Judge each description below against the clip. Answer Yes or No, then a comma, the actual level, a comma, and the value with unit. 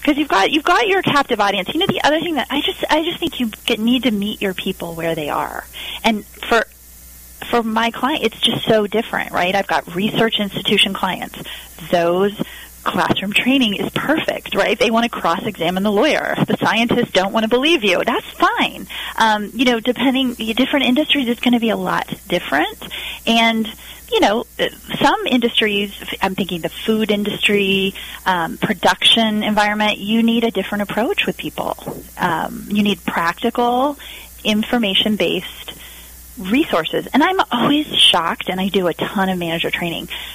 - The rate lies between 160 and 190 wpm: Yes, average, 170 wpm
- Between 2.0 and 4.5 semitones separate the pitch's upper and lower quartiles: Yes, average, 4.2 semitones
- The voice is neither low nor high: No, high, 220 Hz